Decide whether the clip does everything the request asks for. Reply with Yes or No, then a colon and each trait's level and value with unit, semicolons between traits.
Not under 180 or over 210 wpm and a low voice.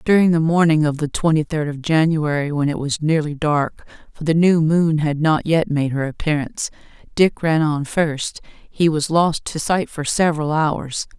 No: average, 195 wpm; medium, 155 Hz